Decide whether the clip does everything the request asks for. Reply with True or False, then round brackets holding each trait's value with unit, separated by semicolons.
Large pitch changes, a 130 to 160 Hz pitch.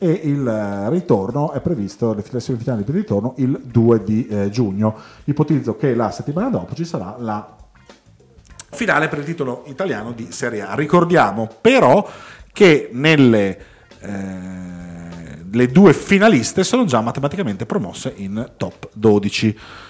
False (6.0 semitones; 120 Hz)